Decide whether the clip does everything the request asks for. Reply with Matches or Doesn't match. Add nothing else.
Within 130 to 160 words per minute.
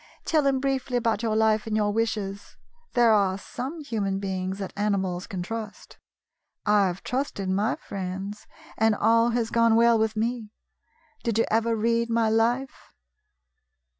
Matches